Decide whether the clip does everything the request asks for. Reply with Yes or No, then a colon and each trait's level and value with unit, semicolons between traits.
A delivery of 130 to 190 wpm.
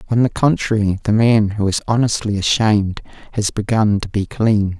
Yes: average, 175 wpm